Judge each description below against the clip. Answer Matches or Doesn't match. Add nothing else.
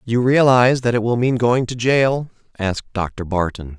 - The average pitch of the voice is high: Doesn't match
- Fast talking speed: Doesn't match